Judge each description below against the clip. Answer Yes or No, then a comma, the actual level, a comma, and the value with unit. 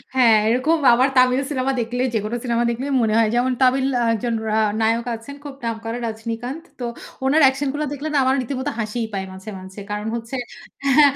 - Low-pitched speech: No, high, 245 Hz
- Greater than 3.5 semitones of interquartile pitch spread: No, average, 3.0 semitones